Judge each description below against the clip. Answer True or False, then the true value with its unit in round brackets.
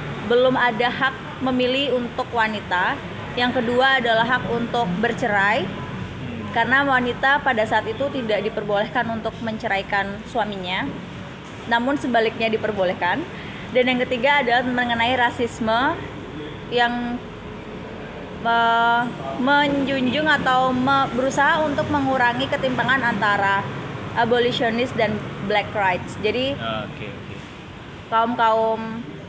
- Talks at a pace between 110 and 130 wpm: False (100 wpm)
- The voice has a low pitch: False (240 Hz)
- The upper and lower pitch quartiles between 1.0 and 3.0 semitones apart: True (2.5 semitones)